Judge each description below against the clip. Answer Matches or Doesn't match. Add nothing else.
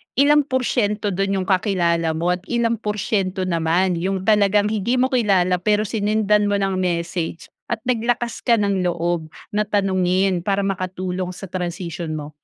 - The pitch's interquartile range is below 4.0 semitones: Matches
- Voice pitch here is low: Doesn't match